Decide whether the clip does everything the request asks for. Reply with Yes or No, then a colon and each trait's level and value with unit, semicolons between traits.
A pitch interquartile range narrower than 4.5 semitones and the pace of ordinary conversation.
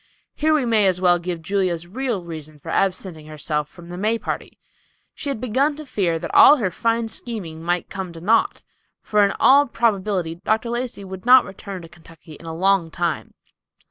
No: average, 5.3 semitones; average, 195 wpm